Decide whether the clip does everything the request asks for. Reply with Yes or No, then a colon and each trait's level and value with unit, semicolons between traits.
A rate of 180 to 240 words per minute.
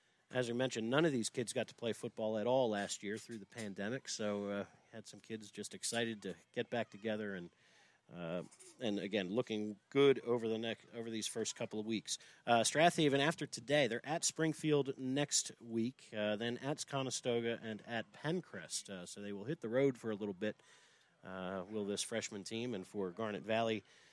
Yes: average, 200 wpm